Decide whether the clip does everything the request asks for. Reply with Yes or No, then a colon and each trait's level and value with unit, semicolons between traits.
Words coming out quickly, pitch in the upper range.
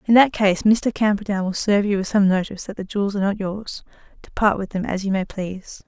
Yes: fast, 245 wpm; high, 200 Hz